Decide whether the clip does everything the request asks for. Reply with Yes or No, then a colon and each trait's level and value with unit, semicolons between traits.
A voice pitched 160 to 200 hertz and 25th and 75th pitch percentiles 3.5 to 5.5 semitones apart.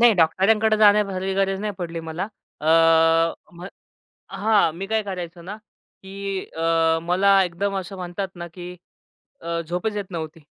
No: high, 190 Hz; average, 2.8 semitones